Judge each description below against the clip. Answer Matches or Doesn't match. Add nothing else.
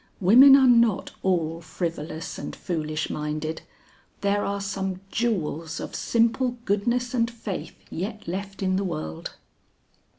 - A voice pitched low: Doesn't match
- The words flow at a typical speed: Doesn't match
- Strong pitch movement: Matches